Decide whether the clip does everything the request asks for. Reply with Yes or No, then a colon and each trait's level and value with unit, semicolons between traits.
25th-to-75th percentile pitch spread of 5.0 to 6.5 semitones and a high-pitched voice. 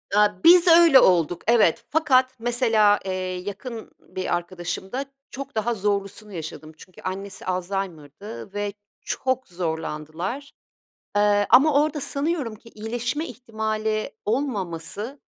Yes: wide, 5.4 semitones; high, 210 Hz